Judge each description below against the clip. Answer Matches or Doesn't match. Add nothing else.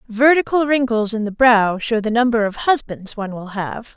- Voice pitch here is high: Matches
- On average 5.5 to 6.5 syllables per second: Doesn't match